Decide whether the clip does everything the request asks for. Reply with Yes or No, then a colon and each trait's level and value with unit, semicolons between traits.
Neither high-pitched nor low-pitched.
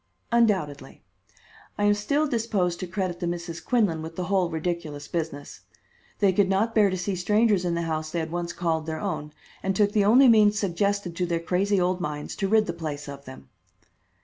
Yes: medium, 180 Hz